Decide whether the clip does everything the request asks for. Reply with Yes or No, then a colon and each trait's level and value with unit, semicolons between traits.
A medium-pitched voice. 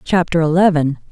Yes: medium, 165 Hz